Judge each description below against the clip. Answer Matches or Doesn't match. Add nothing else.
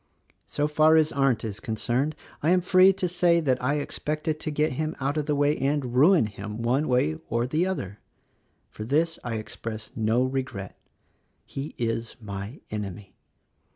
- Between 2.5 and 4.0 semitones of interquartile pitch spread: Doesn't match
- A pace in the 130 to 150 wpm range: Doesn't match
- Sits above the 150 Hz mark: Doesn't match